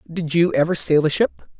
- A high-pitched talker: No, medium, 150 Hz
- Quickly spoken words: Yes, fast, 225 wpm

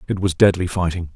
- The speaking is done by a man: Yes, male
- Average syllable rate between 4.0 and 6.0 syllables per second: No, 6.2 syllables/s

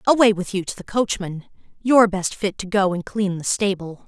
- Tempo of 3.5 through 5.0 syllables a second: No, 5.3 syllables/s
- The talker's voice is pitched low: No, high, 195 Hz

